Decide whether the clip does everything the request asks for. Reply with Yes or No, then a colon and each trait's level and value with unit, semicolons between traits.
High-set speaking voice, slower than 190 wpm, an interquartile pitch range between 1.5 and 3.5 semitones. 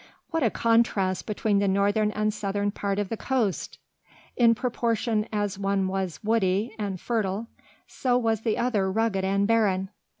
Yes: high, 210 Hz; average, 160 wpm; narrow, 2.6 semitones